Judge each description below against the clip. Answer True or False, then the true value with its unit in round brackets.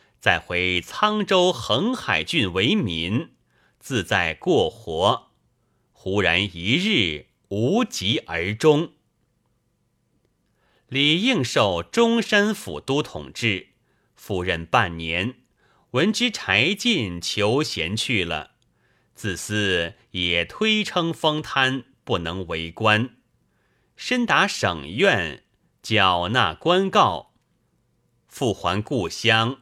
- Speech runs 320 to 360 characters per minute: False (130 characters per minute)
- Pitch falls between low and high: False (120 Hz)